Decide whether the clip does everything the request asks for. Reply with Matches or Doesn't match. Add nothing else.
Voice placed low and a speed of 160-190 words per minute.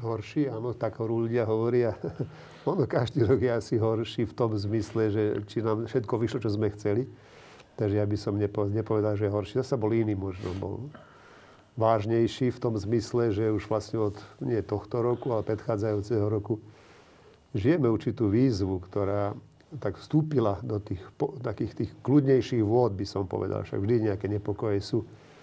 Matches